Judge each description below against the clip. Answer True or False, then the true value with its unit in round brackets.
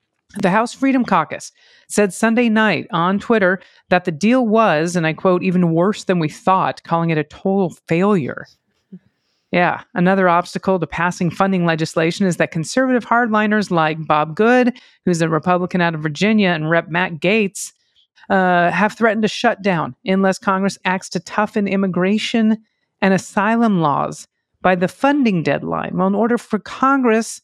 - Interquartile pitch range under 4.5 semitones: True (3.7 semitones)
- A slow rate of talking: False (160 wpm)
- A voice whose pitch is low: False (190 Hz)